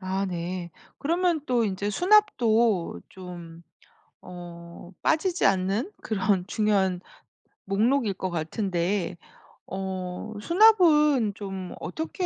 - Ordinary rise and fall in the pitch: No, wide, 6.2 semitones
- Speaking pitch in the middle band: No, high, 195 Hz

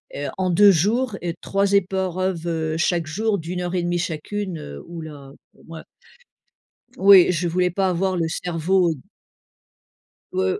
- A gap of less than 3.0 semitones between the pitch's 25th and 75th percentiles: Yes, narrow, 2.6 semitones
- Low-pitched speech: No, medium, 175 Hz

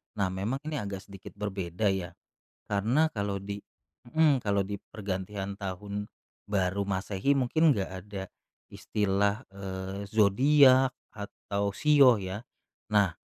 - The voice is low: Yes, low, 100 Hz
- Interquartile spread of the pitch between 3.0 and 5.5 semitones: No, narrow, 2.6 semitones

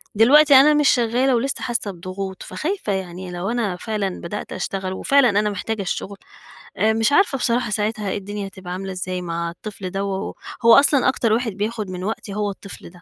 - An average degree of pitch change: Yes, average, 3.7 semitones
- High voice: Yes, high, 205 Hz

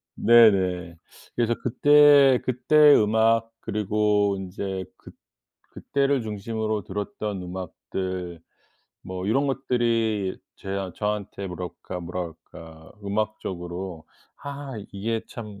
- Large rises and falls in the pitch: No, average, 3.9 semitones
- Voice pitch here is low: Yes, low, 105 Hz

